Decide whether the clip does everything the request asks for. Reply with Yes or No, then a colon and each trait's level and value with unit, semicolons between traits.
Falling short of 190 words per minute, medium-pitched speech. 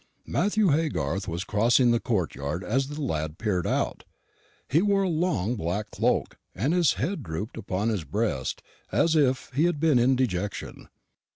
No: average, 165 wpm; low, 120 Hz